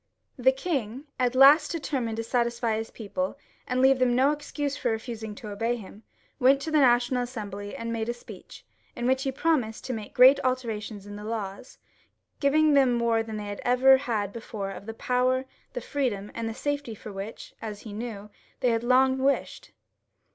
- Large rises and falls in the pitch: No, average, 3.3 semitones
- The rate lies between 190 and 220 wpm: Yes, average, 200 wpm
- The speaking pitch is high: Yes, high, 240 Hz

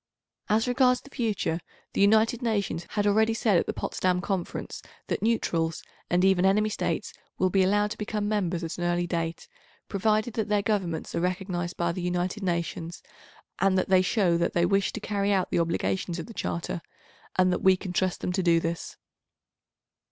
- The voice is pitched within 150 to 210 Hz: Yes, high, 190 Hz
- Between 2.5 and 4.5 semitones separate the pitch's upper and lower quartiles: Yes, average, 3.2 semitones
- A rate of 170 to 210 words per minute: Yes, average, 190 wpm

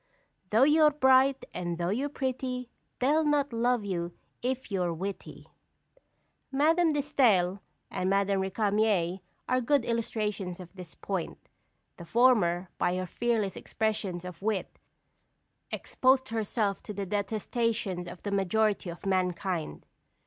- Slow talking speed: Yes, slow, 130 wpm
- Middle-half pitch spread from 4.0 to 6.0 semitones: Yes, wide, 5.5 semitones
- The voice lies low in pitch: No, high, 210 Hz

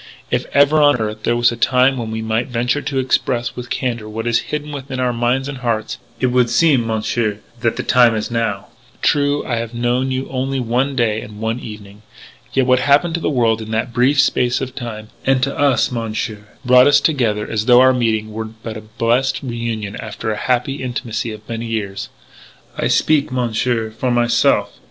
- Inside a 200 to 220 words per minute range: Yes, fast, 205 wpm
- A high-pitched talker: No, low, 120 Hz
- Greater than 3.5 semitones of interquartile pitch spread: No, average, 2.7 semitones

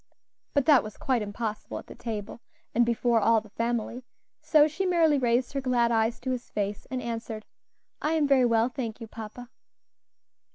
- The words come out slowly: No, average, 180 wpm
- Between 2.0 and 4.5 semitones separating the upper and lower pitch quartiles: Yes, narrow, 2.6 semitones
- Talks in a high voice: Yes, high, 235 Hz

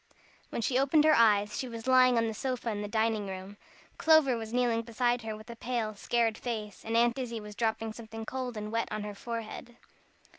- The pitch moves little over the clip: Yes, narrow, 2.2 semitones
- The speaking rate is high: Yes, fast, 215 wpm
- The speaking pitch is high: Yes, high, 230 Hz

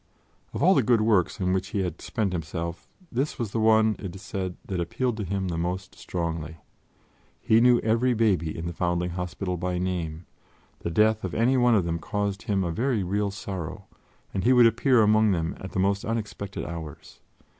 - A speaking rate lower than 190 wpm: No, average, 200 wpm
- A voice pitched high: No, very low, 95 Hz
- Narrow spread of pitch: No, average, 4.0 semitones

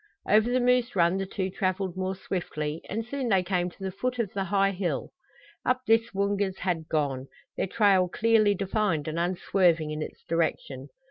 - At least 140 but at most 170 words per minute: No, average, 190 wpm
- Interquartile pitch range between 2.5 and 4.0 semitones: Yes, average, 3.6 semitones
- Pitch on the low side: No, high, 190 Hz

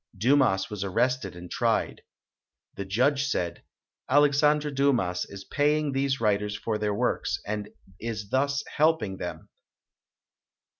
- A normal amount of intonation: No, wide, 5.9 semitones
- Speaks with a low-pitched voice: Yes, low, 115 Hz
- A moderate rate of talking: No, slow, 130 wpm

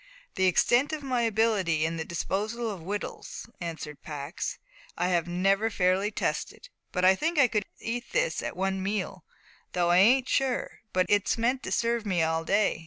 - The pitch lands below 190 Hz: No, high, 195 Hz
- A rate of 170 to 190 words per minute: Yes, average, 175 wpm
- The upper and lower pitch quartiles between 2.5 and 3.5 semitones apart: No, average, 4.8 semitones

